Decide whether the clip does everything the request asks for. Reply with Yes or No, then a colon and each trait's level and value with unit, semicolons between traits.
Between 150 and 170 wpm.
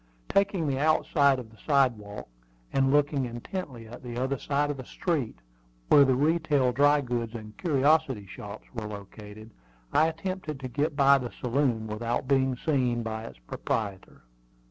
Yes: average, 160 wpm